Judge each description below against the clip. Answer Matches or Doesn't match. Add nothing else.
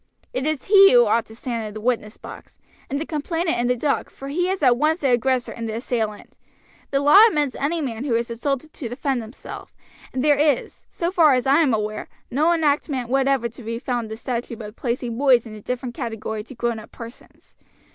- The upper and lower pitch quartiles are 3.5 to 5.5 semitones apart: Matches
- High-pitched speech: Matches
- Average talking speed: Doesn't match